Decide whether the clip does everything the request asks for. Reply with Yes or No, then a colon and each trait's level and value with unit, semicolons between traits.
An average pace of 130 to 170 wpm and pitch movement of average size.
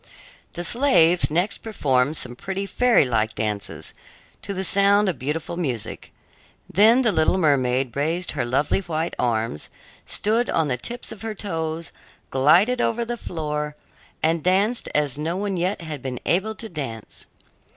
No: average, 155 wpm; wide, 6.7 semitones